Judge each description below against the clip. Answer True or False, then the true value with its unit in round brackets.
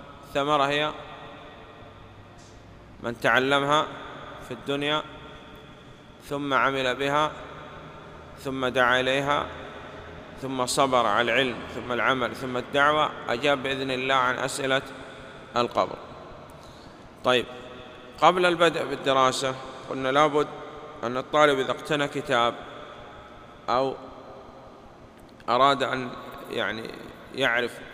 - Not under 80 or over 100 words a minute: True (90 wpm)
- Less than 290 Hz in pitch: True (135 Hz)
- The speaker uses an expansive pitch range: False (2.8 semitones)